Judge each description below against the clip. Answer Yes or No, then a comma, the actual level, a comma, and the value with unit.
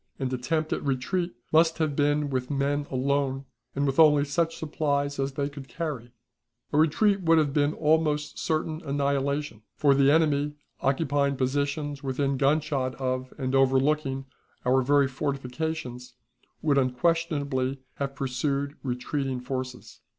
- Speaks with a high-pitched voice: No, medium, 140 Hz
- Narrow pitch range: Yes, narrow, 2.1 semitones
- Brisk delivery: No, slow, 135 wpm